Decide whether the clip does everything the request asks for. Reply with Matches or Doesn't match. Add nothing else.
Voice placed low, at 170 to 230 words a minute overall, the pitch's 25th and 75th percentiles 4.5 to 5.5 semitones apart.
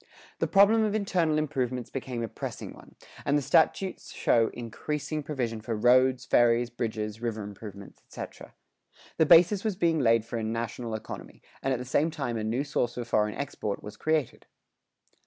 Matches